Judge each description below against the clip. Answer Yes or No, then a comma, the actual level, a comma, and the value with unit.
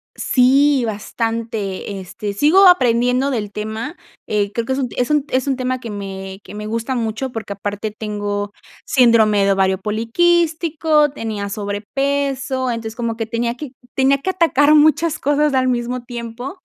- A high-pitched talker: Yes, high, 235 Hz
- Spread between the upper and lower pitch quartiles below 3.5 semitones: No, average, 4.6 semitones